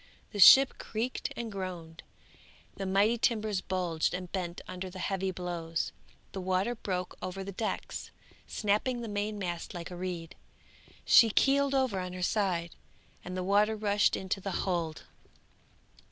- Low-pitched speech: No, high, 190 Hz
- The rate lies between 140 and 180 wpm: Yes, average, 155 wpm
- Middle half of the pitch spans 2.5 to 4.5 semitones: Yes, average, 2.8 semitones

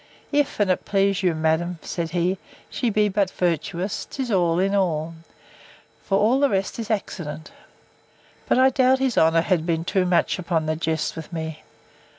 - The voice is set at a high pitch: No, medium, 180 Hz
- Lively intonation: No, average, 3.9 semitones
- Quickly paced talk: No, average, 170 wpm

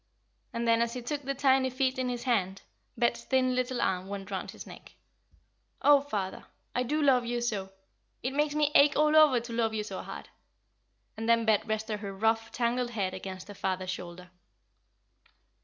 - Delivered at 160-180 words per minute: No, average, 190 wpm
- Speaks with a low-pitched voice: No, high, 235 Hz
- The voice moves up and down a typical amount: Yes, average, 4.3 semitones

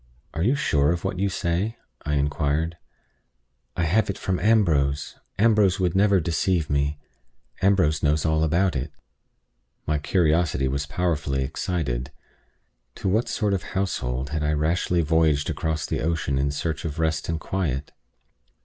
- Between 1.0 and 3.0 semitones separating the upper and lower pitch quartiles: No, average, 4.1 semitones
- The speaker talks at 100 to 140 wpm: No, average, 150 wpm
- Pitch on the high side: No, very low, 80 Hz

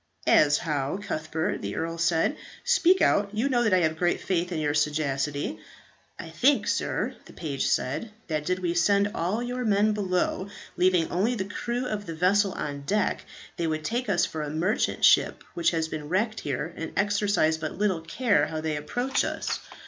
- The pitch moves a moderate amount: Yes, average, 4.8 semitones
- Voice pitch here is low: No, medium, 175 Hz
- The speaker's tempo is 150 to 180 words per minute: No, average, 190 wpm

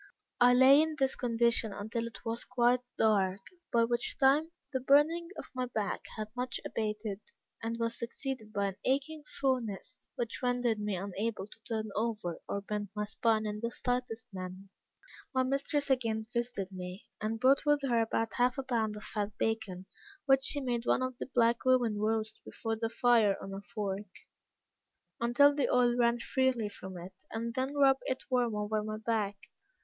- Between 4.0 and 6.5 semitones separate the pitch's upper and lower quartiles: No, average, 3.2 semitones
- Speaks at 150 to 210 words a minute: Yes, average, 180 wpm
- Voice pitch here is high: Yes, high, 230 Hz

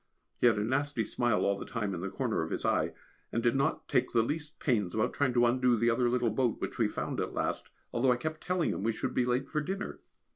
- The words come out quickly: Yes, fast, 260 wpm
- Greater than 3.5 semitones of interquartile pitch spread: No, average, 3.0 semitones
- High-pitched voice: No, low, 120 Hz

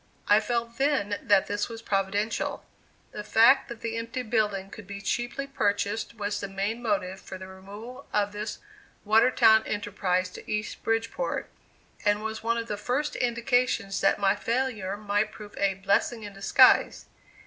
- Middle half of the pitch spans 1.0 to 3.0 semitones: Yes, narrow, 2.5 semitones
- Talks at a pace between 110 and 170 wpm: Yes, average, 160 wpm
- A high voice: Yes, high, 210 Hz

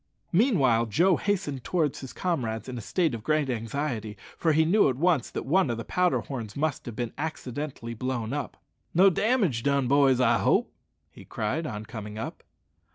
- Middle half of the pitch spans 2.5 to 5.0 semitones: No, wide, 5.6 semitones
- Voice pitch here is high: No, low, 135 Hz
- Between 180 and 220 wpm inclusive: Yes, average, 185 wpm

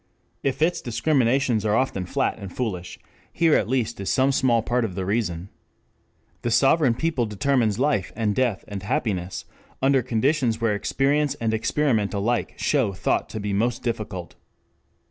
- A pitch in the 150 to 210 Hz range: No, low, 115 Hz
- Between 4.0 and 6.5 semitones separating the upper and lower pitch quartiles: Yes, average, 4.5 semitones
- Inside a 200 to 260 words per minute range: No, average, 160 wpm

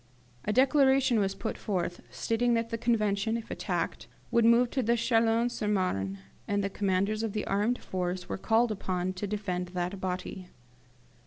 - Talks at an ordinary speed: Yes, average, 165 wpm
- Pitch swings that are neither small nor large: Yes, average, 3.8 semitones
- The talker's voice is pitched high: Yes, high, 210 Hz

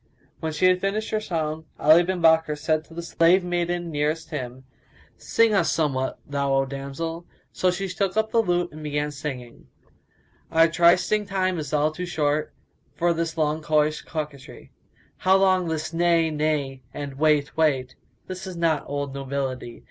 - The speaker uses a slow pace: No, average, 175 wpm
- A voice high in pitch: No, medium, 160 Hz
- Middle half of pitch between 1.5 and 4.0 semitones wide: Yes, average, 3.2 semitones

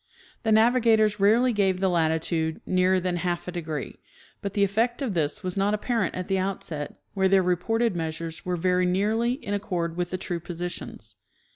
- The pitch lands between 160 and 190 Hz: Yes, medium, 185 Hz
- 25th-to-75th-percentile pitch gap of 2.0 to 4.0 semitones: Yes, average, 3.2 semitones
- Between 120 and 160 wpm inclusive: No, average, 180 wpm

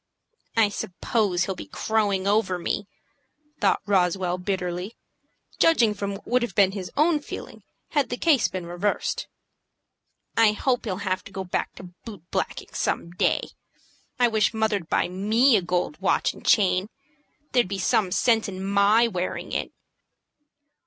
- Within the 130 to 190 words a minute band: Yes, average, 155 wpm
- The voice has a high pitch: Yes, high, 200 Hz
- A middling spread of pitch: Yes, average, 3.2 semitones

